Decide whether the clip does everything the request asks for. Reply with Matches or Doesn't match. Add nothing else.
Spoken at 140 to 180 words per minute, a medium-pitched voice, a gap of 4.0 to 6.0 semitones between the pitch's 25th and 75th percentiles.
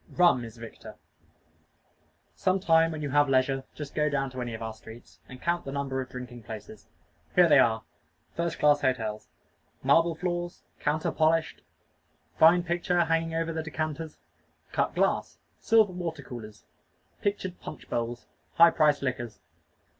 Matches